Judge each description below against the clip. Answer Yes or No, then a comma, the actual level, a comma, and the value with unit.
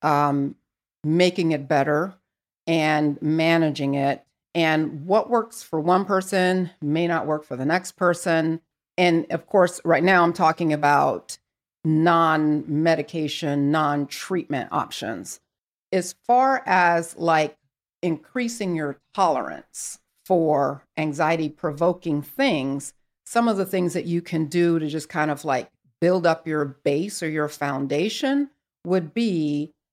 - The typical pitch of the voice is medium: Yes, medium, 160 Hz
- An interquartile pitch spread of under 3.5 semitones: Yes, average, 3.0 semitones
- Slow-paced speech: Yes, slow, 130 wpm